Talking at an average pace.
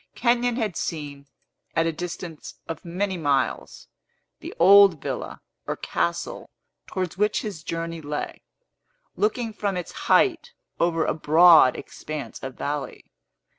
No: slow, 130 wpm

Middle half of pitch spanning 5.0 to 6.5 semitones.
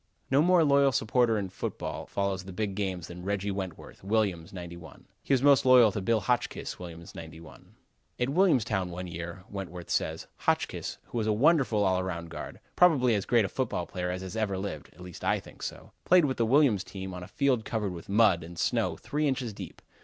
Yes: wide, 5.4 semitones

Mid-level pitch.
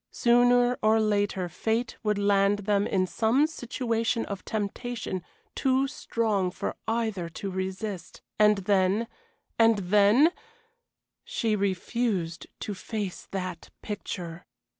No: high, 210 Hz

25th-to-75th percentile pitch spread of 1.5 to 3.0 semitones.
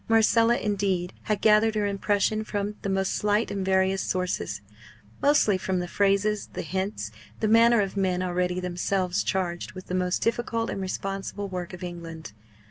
Yes: narrow, 2.6 semitones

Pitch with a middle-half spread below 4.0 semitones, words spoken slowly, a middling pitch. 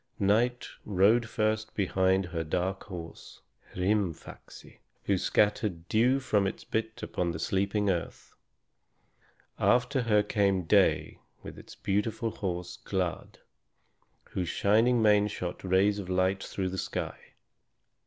No: average, 2.8 semitones; slow, 125 wpm; low, 100 Hz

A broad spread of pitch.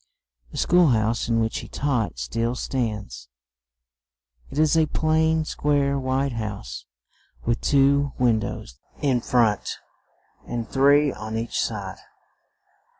No: average, 4.5 semitones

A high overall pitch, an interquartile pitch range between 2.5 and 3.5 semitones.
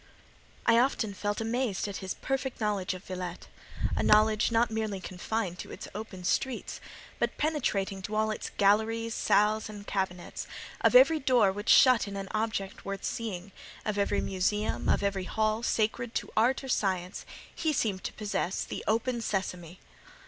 Yes: high, 210 Hz; average, 2.8 semitones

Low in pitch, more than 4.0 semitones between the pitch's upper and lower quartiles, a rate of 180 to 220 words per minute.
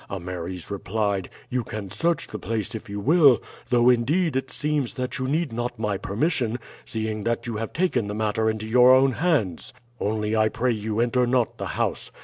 No: low, 115 Hz; average, 3.3 semitones; average, 190 wpm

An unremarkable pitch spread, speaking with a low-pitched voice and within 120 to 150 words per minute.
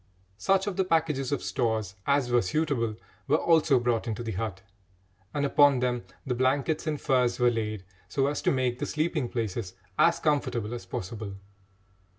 No: average, 4.3 semitones; low, 125 Hz; average, 170 wpm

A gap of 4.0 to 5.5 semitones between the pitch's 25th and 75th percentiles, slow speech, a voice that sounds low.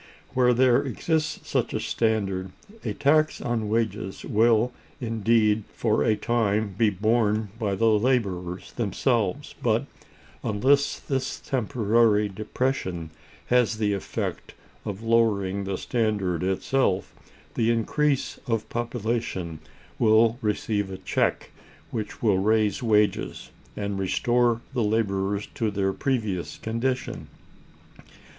No: average, 2.9 semitones; slow, 115 wpm; low, 110 Hz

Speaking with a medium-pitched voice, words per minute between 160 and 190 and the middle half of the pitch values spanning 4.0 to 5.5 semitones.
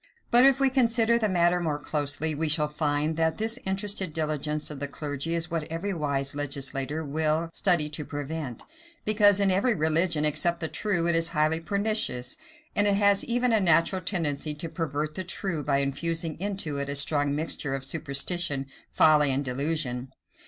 Yes: medium, 160 Hz; average, 180 wpm; average, 4.3 semitones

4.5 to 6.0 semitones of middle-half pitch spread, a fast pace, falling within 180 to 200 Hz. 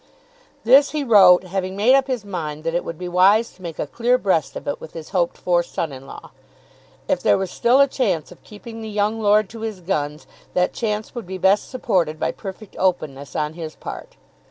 Yes: average, 4.8 semitones; fast, 220 wpm; high, 190 Hz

